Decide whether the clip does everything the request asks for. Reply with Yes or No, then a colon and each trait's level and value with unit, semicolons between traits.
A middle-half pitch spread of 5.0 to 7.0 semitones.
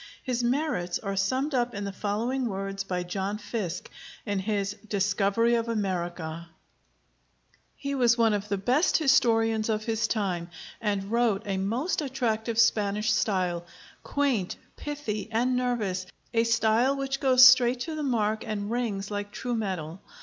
No: average, 3.7 semitones